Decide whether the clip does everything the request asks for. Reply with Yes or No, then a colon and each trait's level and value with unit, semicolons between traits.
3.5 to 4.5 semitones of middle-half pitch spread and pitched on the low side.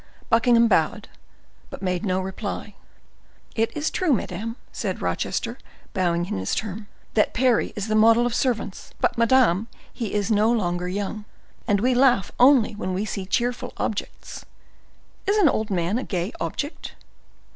No: average, 3.9 semitones; high, 215 Hz